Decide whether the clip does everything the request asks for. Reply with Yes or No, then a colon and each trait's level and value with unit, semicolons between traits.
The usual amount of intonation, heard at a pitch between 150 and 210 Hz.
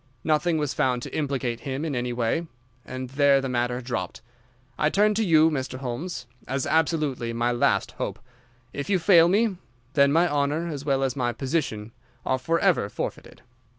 No: average, 4.5 semitones; medium, 140 Hz